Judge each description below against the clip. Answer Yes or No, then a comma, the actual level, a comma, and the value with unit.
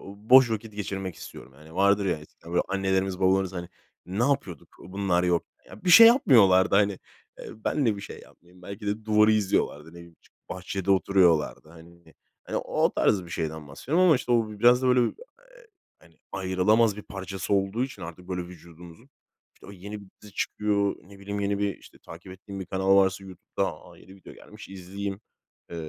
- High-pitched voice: No, very low, 95 Hz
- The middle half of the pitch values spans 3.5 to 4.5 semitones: No, average, 2.9 semitones